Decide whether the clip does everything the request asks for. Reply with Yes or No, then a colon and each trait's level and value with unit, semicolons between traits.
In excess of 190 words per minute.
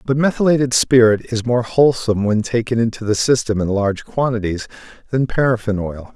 No: average, 165 wpm